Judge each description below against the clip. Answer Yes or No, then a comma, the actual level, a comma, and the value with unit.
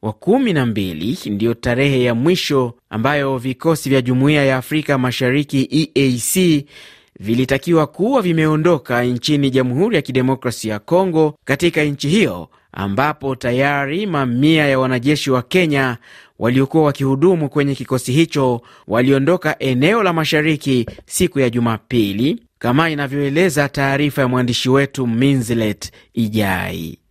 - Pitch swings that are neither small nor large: Yes, average, 3.7 semitones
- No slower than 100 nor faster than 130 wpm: Yes, average, 120 wpm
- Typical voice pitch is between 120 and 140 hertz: Yes, low, 135 Hz